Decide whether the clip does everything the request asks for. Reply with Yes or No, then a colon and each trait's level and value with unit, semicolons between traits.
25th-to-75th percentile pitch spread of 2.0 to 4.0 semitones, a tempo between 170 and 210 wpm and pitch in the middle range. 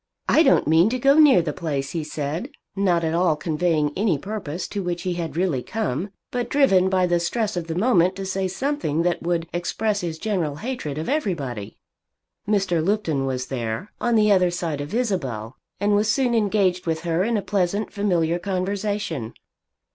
No: average, 4.5 semitones; average, 185 wpm; medium, 180 Hz